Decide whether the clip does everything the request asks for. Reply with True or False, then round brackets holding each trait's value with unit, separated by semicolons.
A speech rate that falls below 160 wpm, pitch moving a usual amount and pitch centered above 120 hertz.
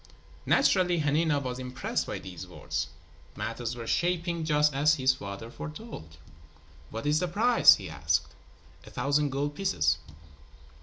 False (140 wpm; 5.9 semitones; 140 Hz)